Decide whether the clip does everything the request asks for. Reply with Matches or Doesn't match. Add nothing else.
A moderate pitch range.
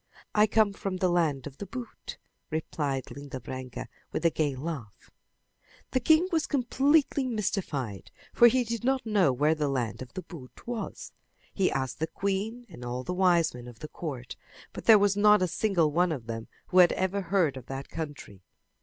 Doesn't match